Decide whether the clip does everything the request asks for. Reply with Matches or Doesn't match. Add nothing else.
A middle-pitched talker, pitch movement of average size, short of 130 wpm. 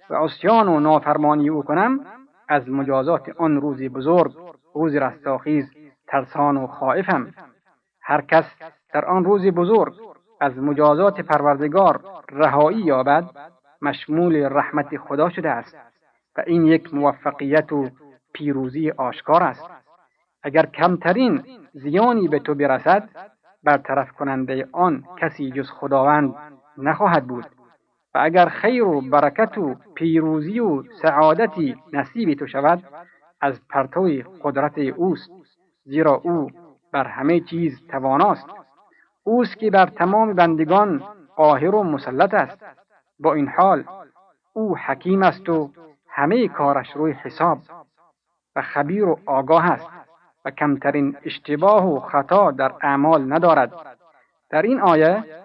Matches